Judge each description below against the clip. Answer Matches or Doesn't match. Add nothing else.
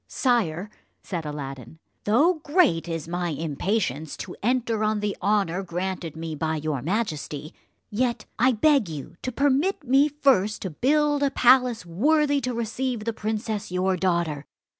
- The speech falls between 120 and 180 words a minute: Matches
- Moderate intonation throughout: Doesn't match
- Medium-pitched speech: Doesn't match